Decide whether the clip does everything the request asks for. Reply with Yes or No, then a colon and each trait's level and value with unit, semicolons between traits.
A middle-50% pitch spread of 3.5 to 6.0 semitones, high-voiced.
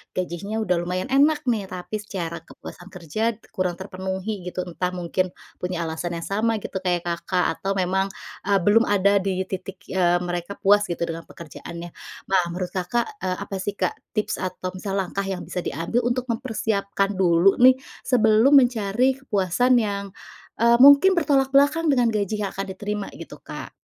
Yes: average, 3.9 semitones; high, 195 Hz